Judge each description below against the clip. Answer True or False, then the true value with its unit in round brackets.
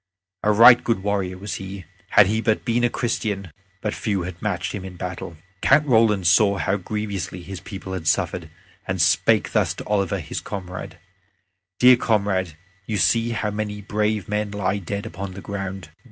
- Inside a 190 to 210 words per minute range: False (180 wpm)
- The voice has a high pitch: False (100 Hz)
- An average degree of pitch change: False (2.3 semitones)